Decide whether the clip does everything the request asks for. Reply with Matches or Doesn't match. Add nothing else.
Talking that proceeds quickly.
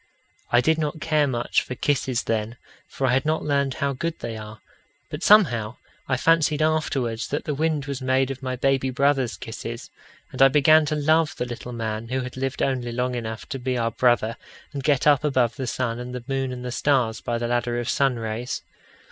Matches